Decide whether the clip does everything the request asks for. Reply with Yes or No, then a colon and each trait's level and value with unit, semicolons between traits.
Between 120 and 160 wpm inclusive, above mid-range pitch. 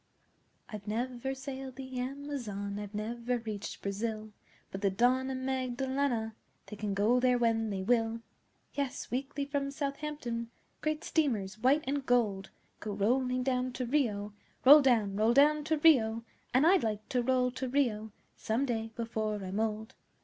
Yes: average, 155 wpm; high, 245 Hz